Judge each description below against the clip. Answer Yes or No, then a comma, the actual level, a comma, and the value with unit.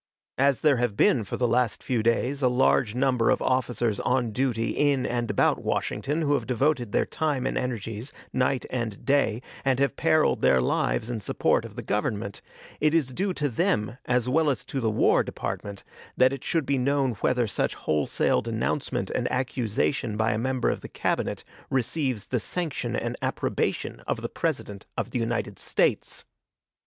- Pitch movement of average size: Yes, average, 3.3 semitones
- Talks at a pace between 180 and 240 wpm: Yes, average, 185 wpm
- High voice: No, low, 125 Hz